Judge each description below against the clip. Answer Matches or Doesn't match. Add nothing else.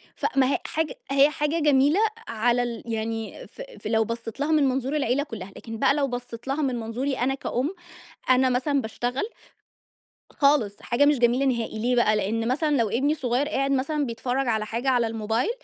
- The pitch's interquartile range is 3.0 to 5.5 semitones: Matches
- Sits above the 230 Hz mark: Matches